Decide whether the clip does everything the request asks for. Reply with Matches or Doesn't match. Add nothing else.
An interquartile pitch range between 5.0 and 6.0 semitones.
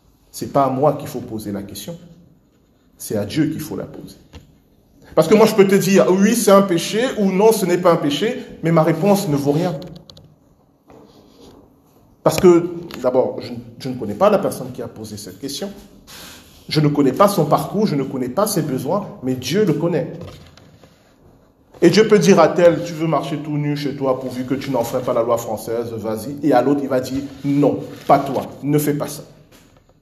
Matches